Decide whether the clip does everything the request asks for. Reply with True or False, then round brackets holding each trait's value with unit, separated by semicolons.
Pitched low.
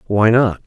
True (110 Hz)